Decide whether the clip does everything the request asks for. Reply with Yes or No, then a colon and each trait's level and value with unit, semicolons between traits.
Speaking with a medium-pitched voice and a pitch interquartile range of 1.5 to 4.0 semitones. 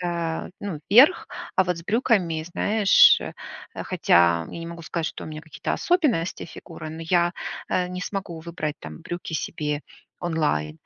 Yes: medium, 170 Hz; average, 2.8 semitones